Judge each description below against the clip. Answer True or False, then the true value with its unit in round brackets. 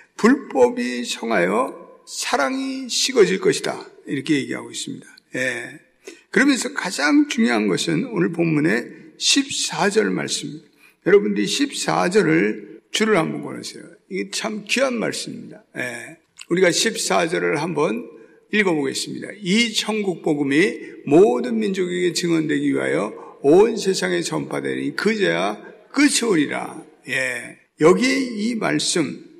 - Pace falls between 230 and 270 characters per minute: True (265 characters per minute)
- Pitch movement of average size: False (7.4 semitones)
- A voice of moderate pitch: False (235 Hz)